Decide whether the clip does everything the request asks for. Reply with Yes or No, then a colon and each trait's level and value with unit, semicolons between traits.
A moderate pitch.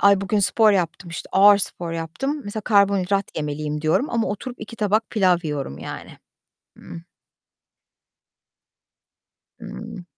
No: high, 195 Hz